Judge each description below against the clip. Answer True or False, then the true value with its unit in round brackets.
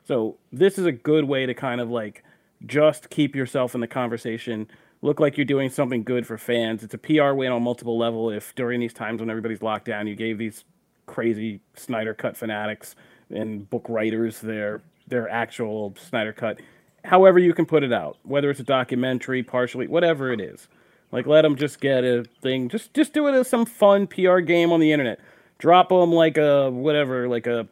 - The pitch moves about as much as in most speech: True (4.9 semitones)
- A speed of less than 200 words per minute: False (205 wpm)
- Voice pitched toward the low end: True (125 Hz)